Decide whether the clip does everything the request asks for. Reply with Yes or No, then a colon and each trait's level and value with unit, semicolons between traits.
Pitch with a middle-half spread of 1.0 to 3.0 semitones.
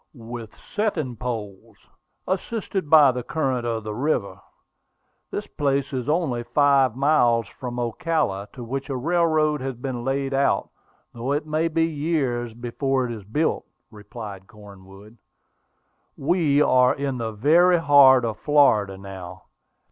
No: average, 4.5 semitones